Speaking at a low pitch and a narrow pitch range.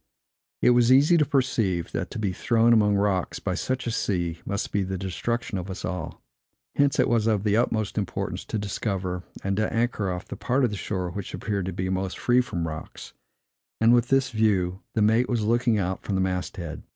No: low, 105 Hz; average, 4.0 semitones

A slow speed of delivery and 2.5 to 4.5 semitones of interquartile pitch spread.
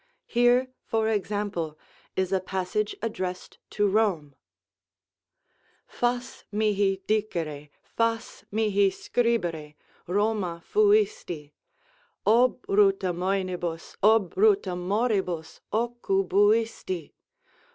Yes: slow, 75 wpm; average, 3.6 semitones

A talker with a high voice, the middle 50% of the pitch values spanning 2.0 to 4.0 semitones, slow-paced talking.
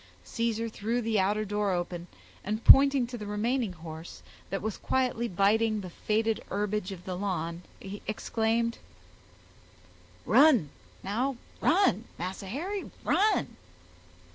Yes: high, 215 Hz; average, 3.6 semitones; slow, 115 wpm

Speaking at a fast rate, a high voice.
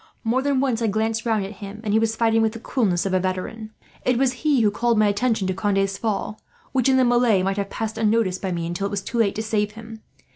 Yes: fast, 265 wpm; high, 220 Hz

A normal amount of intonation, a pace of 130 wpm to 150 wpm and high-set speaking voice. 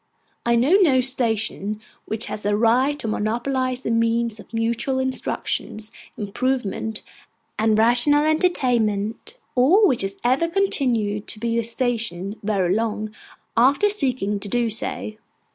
Yes: average, 3.4 semitones; slow, 135 wpm; high, 230 Hz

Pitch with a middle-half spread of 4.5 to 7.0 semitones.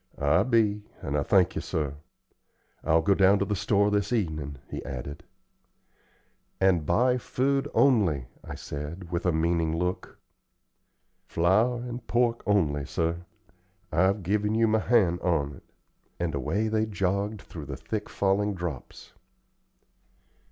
Yes: average, 4.8 semitones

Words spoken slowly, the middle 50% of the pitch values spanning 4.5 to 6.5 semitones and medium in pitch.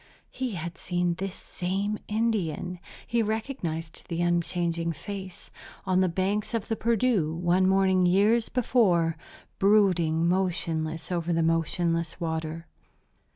No: slow, 120 wpm; average, 3.3 semitones; medium, 180 Hz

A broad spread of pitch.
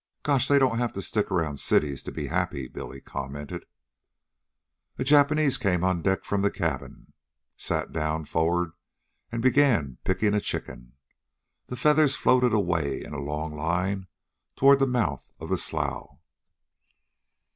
Yes: wide, 8.5 semitones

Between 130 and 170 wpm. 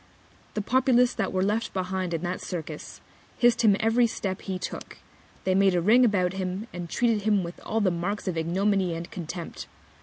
No: average, 190 wpm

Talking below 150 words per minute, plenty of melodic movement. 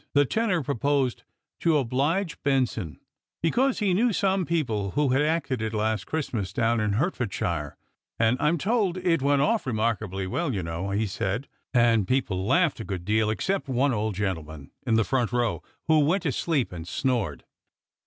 No: average, 180 wpm; wide, 7.0 semitones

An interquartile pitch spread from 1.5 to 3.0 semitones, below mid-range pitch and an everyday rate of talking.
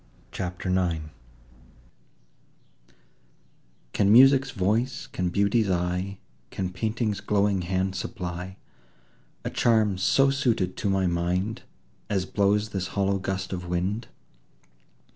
No: narrow, 2.6 semitones; very low, 95 Hz; slow, 105 wpm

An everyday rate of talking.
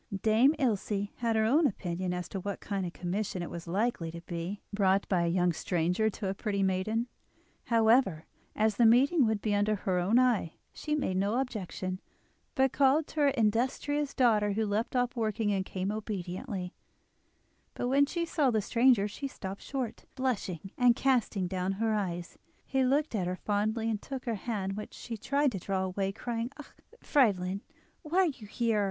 Yes: average, 185 wpm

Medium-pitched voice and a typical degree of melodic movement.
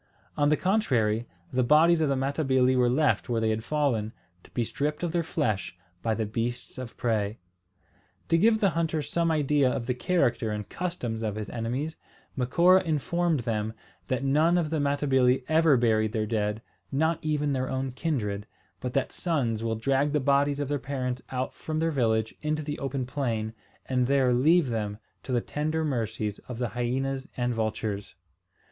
No: low, 130 Hz; average, 4.8 semitones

